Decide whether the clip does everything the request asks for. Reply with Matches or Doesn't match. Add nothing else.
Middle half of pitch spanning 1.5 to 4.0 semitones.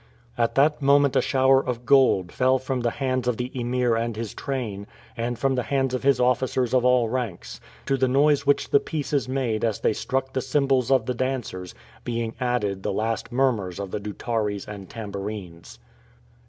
Matches